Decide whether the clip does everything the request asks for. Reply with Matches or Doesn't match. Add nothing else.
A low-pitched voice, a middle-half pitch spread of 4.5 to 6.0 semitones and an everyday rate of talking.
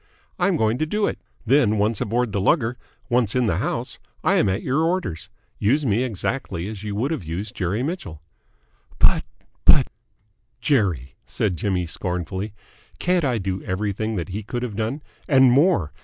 Matches